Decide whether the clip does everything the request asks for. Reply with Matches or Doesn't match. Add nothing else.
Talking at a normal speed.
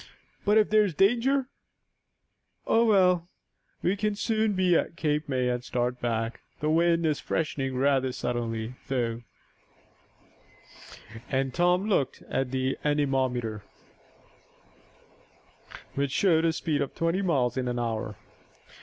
Doesn't match